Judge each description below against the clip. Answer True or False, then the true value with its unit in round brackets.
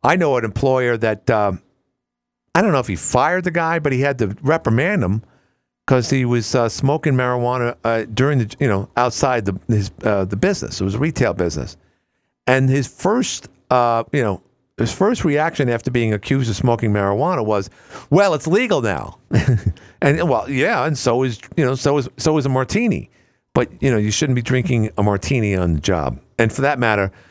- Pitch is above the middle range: False (120 Hz)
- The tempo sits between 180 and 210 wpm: True (200 wpm)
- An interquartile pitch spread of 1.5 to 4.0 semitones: False (4.5 semitones)